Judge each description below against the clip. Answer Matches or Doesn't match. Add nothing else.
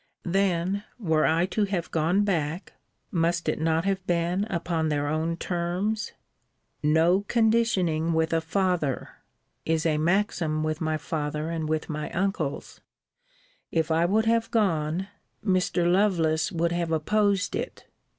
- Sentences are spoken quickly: Doesn't match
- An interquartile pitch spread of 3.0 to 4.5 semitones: Matches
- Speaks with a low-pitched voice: Doesn't match